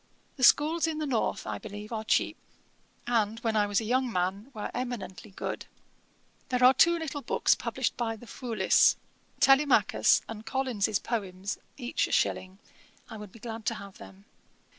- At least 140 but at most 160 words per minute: No, average, 170 wpm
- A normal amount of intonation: Yes, average, 3.9 semitones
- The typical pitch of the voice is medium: No, high, 225 Hz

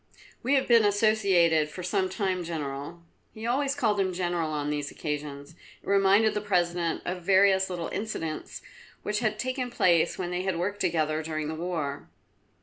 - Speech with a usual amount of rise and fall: Yes, average, 4.3 semitones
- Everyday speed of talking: Yes, average, 170 wpm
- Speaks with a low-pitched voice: No, medium, 180 Hz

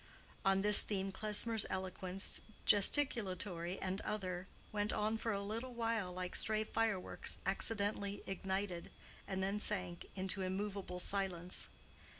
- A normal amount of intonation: No, narrow, 2.2 semitones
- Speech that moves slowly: Yes, slow, 125 wpm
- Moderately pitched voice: No, high, 195 Hz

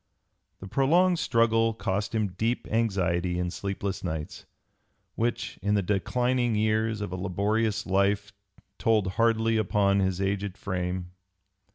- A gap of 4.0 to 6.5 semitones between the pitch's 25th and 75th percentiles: No, average, 3.2 semitones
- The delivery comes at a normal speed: No, slow, 130 wpm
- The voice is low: Yes, low, 105 Hz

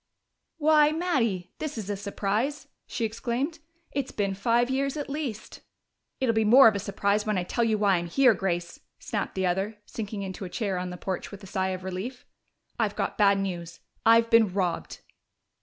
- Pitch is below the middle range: No, high, 210 Hz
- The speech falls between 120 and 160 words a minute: No, average, 195 wpm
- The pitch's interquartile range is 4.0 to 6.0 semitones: Yes, average, 4.3 semitones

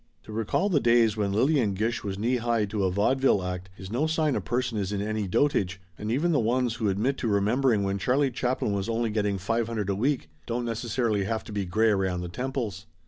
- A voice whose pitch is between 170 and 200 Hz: No, low, 110 Hz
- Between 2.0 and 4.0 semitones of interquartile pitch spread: Yes, average, 3.7 semitones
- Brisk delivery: Yes, fast, 235 wpm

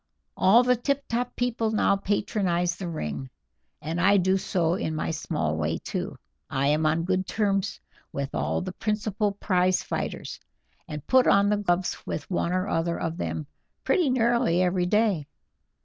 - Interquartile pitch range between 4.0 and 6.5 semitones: Yes, average, 4.4 semitones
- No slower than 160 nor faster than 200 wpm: Yes, average, 165 wpm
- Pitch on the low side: No, medium, 185 Hz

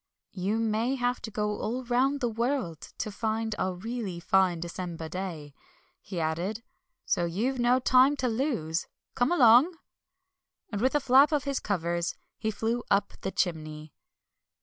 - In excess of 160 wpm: No, average, 155 wpm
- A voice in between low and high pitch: No, high, 220 Hz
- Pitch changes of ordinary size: No, wide, 5.8 semitones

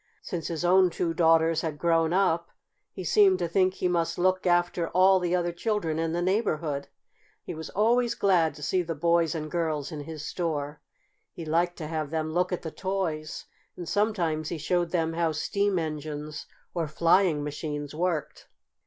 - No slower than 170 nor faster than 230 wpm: Yes, average, 180 wpm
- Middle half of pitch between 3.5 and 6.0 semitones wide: No, narrow, 2.5 semitones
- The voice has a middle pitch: Yes, medium, 170 Hz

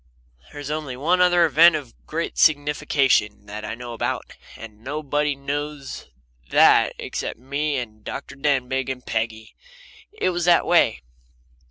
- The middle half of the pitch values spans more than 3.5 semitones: Yes, average, 4.1 semitones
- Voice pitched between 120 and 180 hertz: Yes, medium, 140 Hz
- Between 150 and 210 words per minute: No, average, 140 wpm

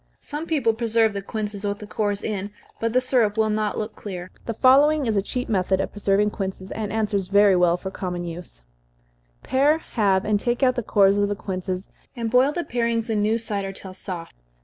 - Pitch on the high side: Yes, high, 210 Hz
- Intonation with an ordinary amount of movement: Yes, average, 3.0 semitones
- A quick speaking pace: Yes, fast, 210 wpm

